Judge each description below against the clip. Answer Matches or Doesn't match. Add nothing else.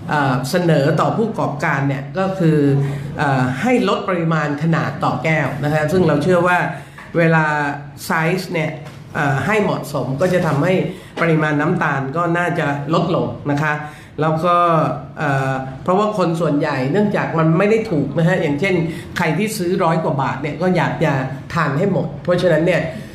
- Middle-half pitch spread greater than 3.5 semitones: Doesn't match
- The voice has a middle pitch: Matches